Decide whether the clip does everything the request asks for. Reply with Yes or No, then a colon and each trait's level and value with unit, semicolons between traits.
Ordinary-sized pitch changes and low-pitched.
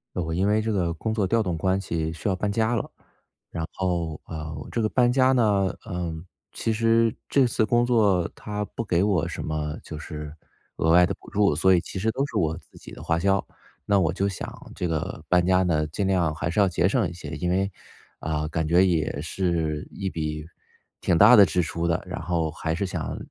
Yes: average, 4.1 semitones; very low, 90 Hz